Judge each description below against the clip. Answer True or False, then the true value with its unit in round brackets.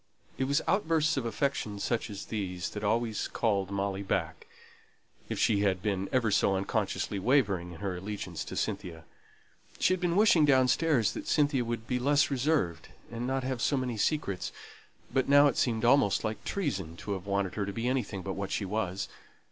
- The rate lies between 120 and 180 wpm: False (190 wpm)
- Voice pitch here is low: True (110 Hz)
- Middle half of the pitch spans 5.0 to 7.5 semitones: True (5.3 semitones)